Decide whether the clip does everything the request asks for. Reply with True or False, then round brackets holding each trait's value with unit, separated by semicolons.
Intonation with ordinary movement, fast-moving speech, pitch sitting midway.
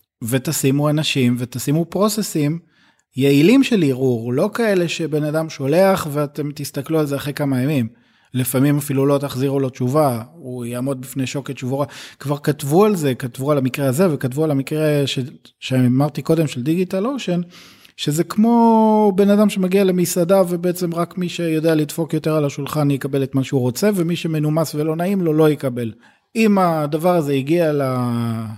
True (4.2 semitones; 160 wpm; 150 Hz)